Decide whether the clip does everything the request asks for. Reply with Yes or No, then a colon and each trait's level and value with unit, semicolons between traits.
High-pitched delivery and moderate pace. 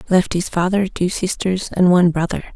No: medium, 180 Hz; average, 190 wpm